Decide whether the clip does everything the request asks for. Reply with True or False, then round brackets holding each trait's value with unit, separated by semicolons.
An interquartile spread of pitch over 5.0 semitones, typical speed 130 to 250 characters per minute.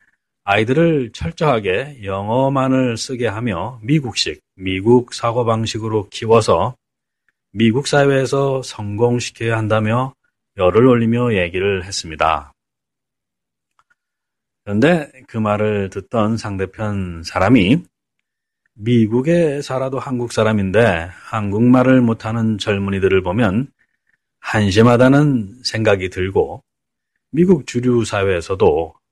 False (3.8 semitones; 235 characters per minute)